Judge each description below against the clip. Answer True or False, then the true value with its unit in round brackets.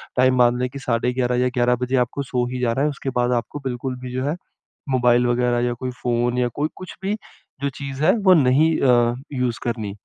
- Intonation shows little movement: True (1.8 semitones)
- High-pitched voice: False (125 Hz)